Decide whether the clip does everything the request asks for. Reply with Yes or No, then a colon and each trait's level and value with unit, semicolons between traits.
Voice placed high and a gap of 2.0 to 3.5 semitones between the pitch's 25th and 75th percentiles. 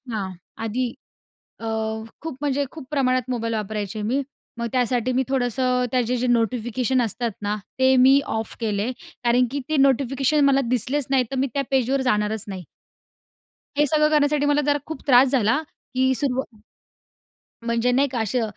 Yes: very high, 255 Hz; average, 3.0 semitones